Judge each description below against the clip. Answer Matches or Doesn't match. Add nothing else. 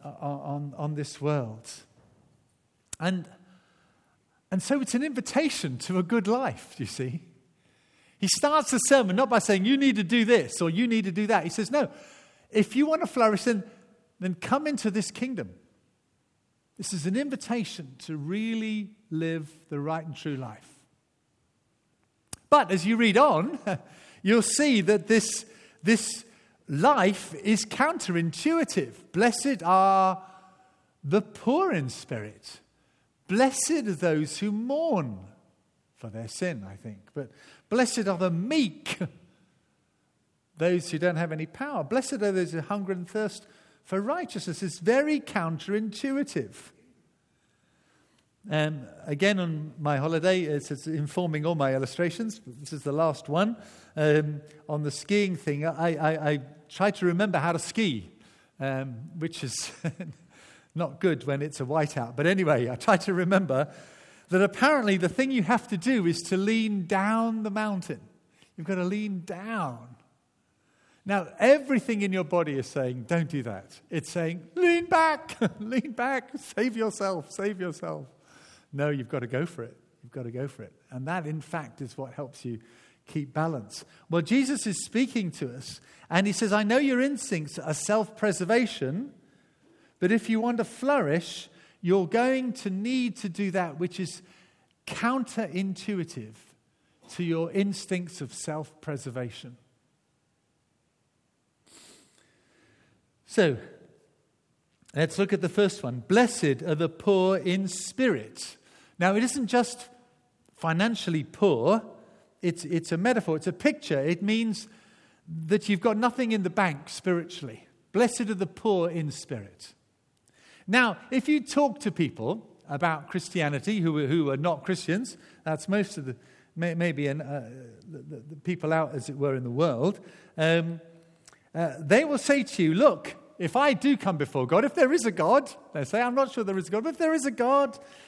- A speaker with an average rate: Matches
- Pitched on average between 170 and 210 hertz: Matches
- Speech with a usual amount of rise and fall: Doesn't match